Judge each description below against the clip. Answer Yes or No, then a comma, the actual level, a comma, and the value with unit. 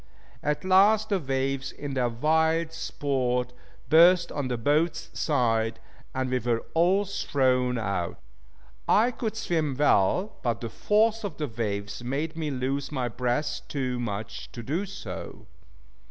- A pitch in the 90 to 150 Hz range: Yes, medium, 140 Hz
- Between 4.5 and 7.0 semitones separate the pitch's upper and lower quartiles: Yes, average, 5.1 semitones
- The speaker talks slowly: No, average, 145 wpm